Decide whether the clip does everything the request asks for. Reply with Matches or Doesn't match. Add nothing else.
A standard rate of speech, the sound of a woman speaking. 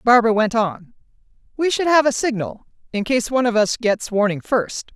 Matches